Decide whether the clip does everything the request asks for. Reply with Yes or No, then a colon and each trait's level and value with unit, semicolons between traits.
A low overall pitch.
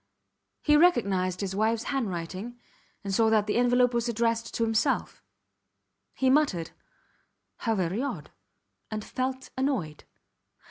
No: high, 230 Hz